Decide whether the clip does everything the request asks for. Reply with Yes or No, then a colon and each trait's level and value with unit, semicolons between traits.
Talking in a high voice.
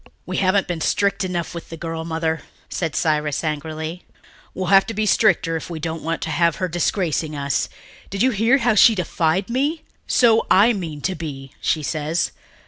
No: medium, 170 Hz